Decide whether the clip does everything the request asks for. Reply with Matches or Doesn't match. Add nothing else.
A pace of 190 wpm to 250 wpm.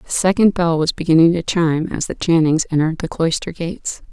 Matches